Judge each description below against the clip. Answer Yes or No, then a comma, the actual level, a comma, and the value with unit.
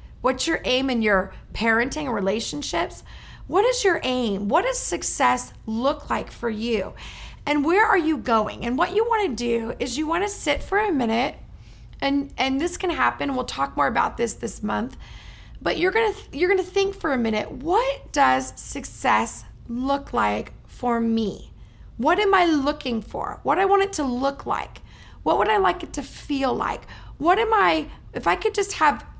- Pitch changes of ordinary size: No, wide, 8.0 semitones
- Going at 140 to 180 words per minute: No, average, 200 wpm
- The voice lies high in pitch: Yes, very high, 280 Hz